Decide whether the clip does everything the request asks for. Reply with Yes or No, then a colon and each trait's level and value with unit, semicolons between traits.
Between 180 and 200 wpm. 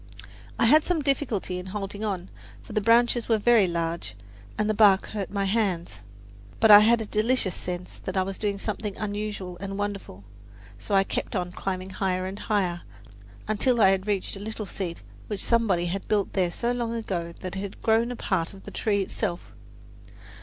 Yes: average, 190 wpm